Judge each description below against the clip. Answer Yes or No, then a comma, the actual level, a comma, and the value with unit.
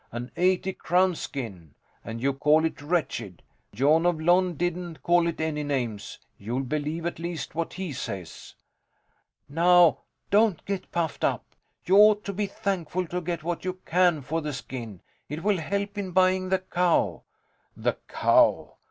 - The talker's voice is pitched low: No, medium, 170 Hz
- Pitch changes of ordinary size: Yes, average, 4.2 semitones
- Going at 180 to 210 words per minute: No, average, 160 wpm